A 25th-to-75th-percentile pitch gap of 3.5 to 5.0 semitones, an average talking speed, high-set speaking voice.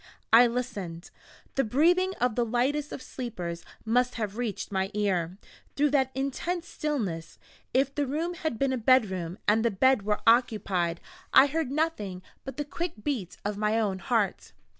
No: wide, 5.5 semitones; average, 165 wpm; high, 240 Hz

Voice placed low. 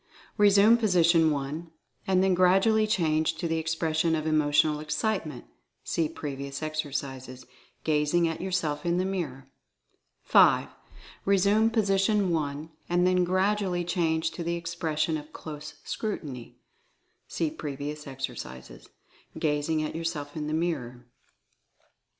No: medium, 160 Hz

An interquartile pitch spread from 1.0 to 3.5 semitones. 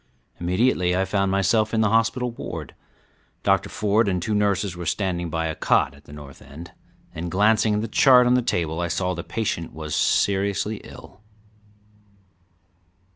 No: average, 4.0 semitones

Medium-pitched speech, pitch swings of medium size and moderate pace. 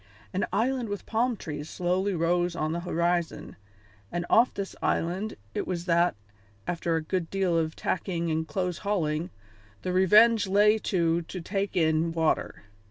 Yes: medium, 175 Hz; average, 3.1 semitones; average, 160 wpm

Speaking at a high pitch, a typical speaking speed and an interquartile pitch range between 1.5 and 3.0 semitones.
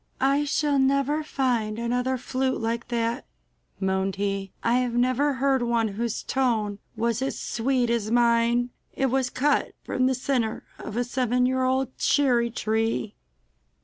Yes: high, 245 Hz; average, 150 wpm; narrow, 2.4 semitones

